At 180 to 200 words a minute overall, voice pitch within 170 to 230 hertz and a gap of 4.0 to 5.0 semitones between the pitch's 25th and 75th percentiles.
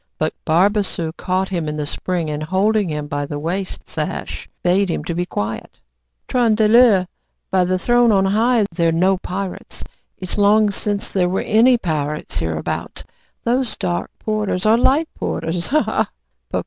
No: average, 160 wpm; high, 190 Hz; average, 4.7 semitones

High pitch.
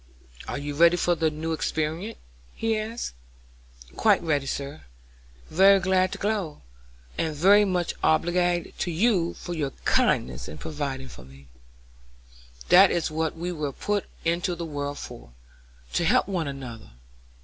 No: medium, 165 Hz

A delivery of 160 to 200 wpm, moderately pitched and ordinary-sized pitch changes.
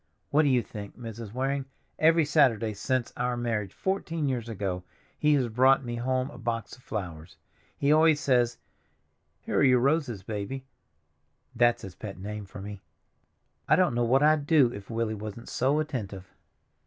No: average, 165 wpm; low, 120 Hz; average, 4.6 semitones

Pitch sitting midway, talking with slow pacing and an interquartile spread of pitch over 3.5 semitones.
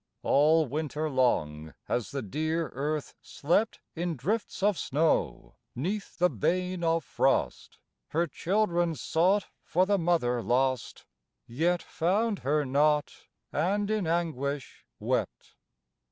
Yes: medium, 160 Hz; slow, 120 wpm; average, 4.7 semitones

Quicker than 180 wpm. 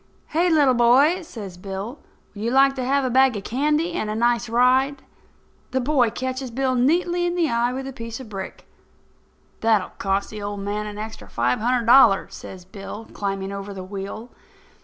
Yes: average, 195 wpm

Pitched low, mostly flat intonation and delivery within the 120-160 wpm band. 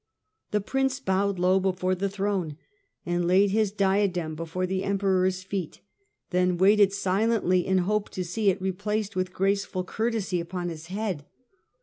No: high, 190 Hz; narrow, 1.8 semitones; average, 150 wpm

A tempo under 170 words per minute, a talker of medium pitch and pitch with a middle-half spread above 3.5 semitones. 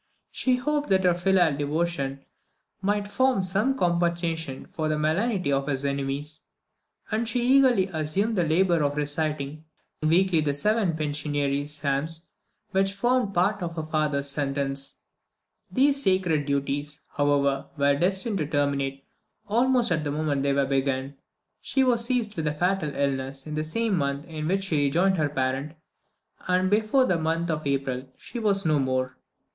Yes: average, 160 wpm; medium, 155 Hz; wide, 5.4 semitones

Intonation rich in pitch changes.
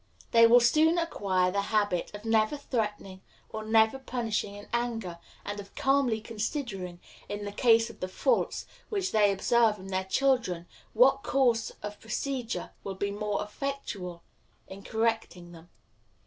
No: average, 3.5 semitones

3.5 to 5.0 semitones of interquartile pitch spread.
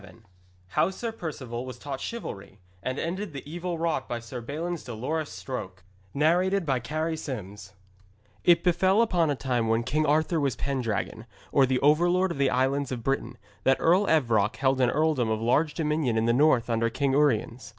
No: wide, 5.4 semitones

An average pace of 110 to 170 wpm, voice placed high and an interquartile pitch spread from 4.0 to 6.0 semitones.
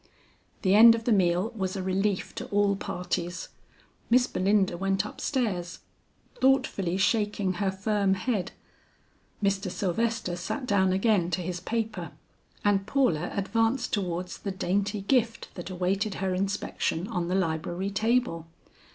No: average, 140 wpm; high, 195 Hz; average, 2.7 semitones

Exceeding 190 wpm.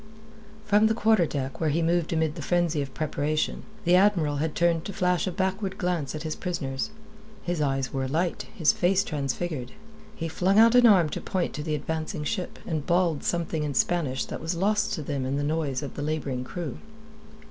Yes: average, 200 wpm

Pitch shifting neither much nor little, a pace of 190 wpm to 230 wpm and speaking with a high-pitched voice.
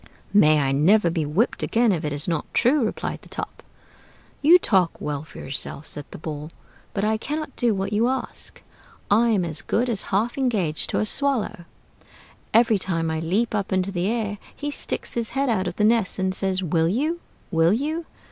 No: wide, 6.1 semitones; average, 200 wpm; high, 200 Hz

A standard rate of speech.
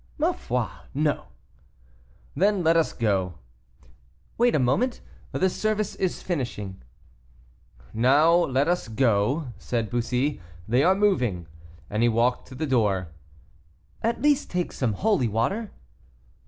No: slow, 130 wpm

